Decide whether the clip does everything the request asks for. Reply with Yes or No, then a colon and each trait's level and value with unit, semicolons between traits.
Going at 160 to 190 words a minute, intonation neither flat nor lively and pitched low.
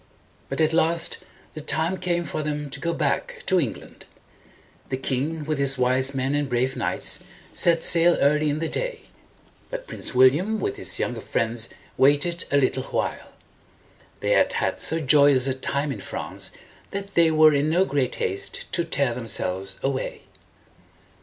No: average, 170 wpm; average, 4.1 semitones; medium, 145 Hz